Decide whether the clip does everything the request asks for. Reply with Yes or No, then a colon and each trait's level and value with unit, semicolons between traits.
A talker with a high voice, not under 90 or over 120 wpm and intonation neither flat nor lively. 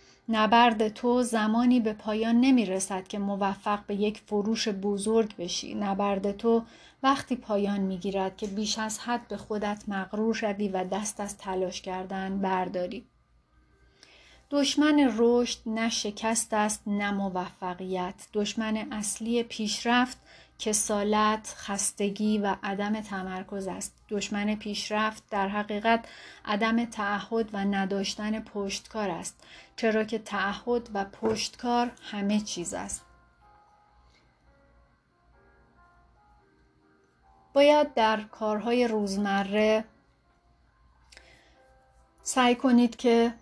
No: high, 210 Hz; slow, 105 wpm; narrow, 2.3 semitones